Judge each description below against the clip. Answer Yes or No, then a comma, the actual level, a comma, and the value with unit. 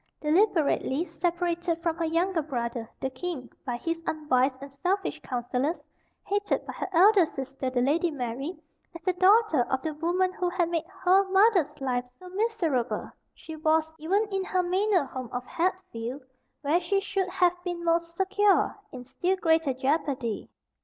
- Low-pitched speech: No, very high, 330 Hz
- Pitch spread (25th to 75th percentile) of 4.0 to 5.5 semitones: Yes, average, 5.2 semitones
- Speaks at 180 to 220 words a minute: No, average, 160 wpm